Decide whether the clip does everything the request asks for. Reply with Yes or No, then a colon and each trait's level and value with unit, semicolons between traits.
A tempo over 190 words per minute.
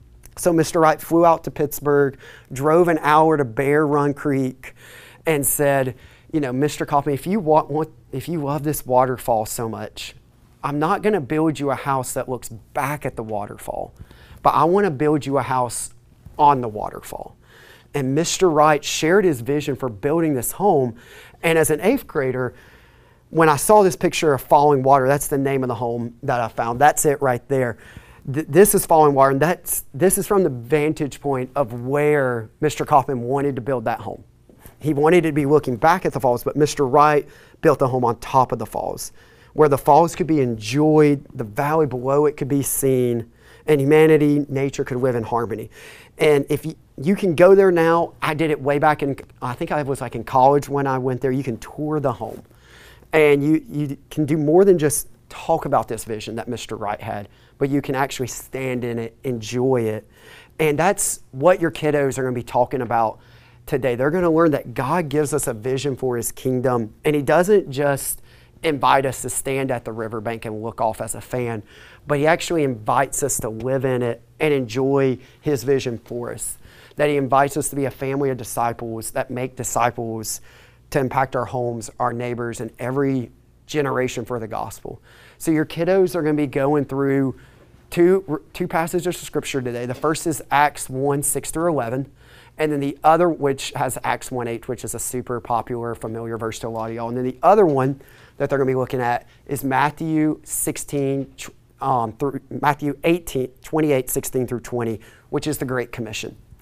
Yes: fast, 205 wpm